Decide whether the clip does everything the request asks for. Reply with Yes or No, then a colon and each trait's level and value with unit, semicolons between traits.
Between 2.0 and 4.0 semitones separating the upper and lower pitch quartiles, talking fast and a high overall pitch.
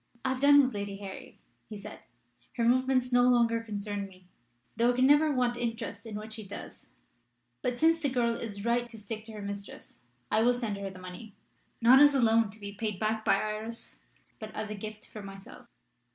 Yes: average, 3.1 semitones; fast, 210 wpm; high, 225 Hz